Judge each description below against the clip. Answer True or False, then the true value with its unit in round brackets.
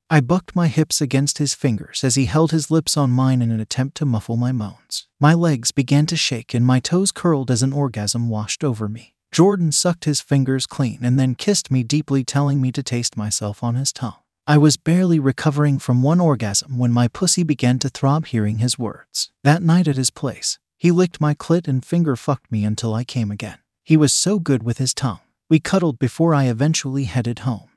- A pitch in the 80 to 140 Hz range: True (135 Hz)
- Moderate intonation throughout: True (4.1 semitones)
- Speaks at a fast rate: True (220 wpm)